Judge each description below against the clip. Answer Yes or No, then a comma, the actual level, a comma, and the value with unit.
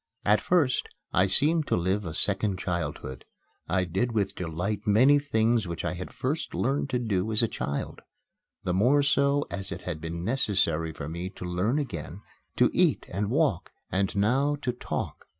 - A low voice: Yes, low, 100 Hz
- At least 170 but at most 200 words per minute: Yes, average, 180 wpm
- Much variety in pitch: Yes, wide, 6.1 semitones